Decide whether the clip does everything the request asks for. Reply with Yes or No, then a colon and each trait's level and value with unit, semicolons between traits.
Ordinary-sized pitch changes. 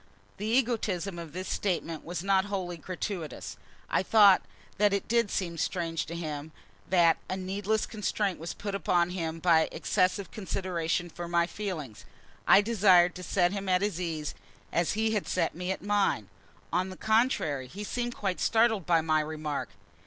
Yes: average, 3.3 semitones